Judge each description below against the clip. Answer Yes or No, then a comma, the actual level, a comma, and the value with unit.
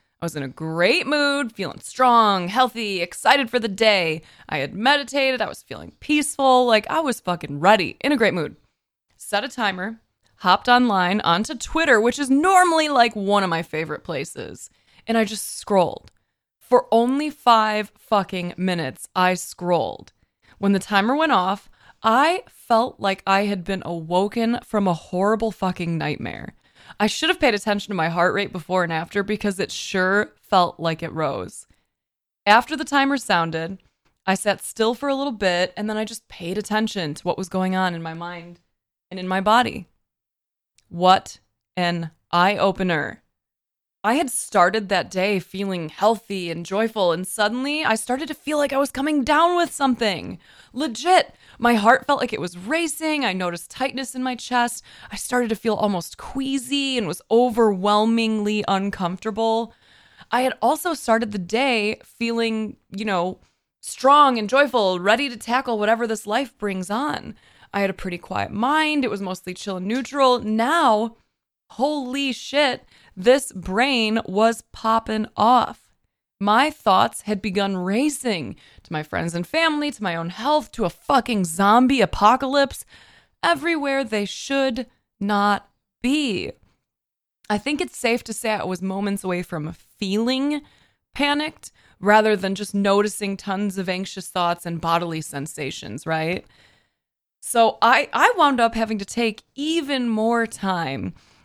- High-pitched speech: Yes, high, 215 Hz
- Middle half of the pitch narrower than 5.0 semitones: No, wide, 5.4 semitones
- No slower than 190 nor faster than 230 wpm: No, average, 160 wpm